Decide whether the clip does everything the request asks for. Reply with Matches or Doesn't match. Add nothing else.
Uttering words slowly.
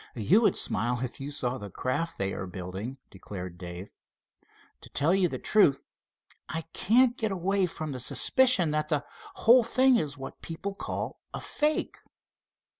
Doesn't match